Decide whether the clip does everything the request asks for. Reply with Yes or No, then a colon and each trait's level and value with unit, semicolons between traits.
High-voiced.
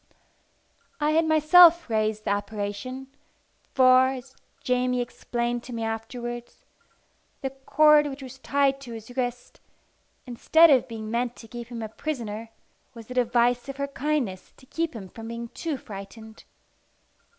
Yes: high, 245 Hz